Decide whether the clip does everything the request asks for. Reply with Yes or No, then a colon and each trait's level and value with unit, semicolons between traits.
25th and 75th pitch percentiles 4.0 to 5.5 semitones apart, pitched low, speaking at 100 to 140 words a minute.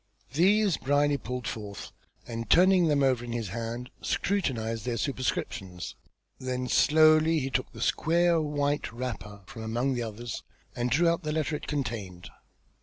No: average, 5.2 semitones; low, 130 Hz; average, 155 wpm